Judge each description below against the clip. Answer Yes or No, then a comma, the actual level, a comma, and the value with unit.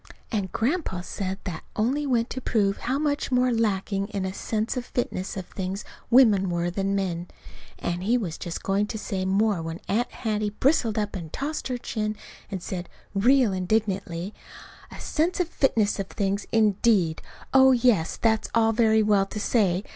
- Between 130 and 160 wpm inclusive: No, average, 175 wpm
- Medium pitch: No, high, 210 Hz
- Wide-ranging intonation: No, average, 3.7 semitones